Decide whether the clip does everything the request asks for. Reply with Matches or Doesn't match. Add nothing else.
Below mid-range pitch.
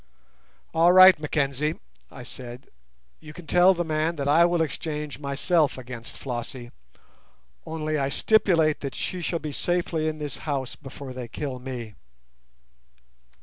Doesn't match